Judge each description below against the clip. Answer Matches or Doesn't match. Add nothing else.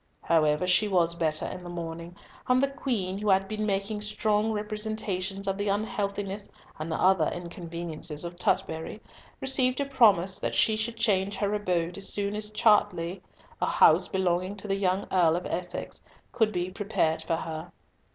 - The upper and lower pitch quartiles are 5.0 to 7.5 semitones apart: Doesn't match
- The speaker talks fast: Doesn't match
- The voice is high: Matches